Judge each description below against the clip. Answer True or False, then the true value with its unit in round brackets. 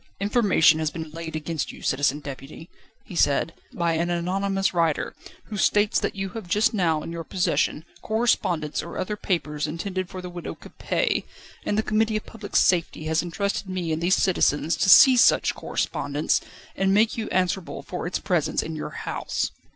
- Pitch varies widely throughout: False (3.7 semitones)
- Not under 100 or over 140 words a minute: False (180 wpm)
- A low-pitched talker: False (175 Hz)